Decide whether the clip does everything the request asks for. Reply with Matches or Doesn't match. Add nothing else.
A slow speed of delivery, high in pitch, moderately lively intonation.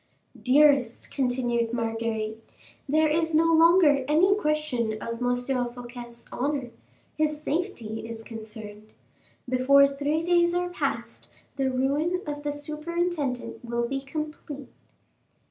Matches